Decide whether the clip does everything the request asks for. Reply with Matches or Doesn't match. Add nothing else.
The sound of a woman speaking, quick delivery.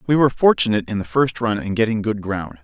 Doesn't match